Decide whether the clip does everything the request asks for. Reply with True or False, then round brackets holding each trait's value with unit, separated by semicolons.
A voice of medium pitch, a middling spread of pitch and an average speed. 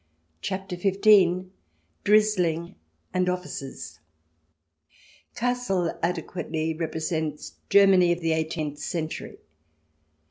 False (175 Hz; 3.2 semitones; 75 wpm)